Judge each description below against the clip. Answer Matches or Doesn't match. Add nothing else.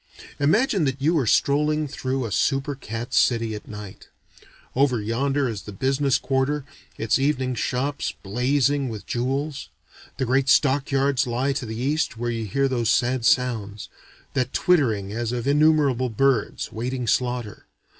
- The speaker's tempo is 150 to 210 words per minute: Matches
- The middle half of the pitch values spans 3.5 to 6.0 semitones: Doesn't match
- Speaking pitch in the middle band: Doesn't match